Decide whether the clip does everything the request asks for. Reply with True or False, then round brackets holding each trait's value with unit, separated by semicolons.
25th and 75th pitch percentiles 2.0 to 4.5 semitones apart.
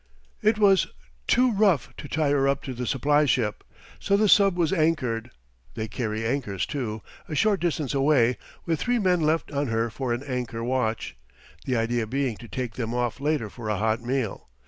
False (5.3 semitones)